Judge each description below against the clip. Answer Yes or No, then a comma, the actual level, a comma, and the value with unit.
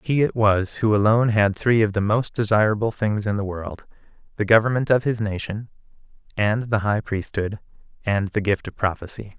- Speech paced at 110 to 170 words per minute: No, average, 180 wpm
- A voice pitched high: No, low, 105 Hz